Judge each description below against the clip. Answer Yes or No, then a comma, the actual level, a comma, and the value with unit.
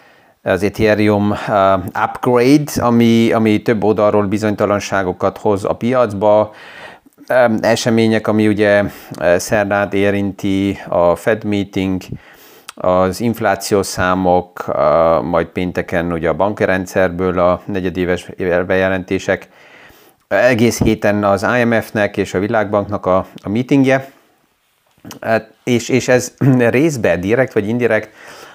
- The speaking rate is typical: No, slow, 100 wpm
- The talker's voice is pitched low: Yes, low, 105 Hz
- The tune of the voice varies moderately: Yes, average, 3.0 semitones